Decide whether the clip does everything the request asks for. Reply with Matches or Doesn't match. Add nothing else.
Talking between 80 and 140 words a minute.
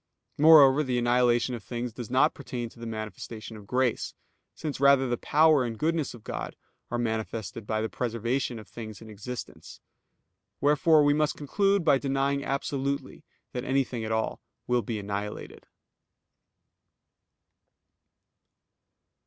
Matches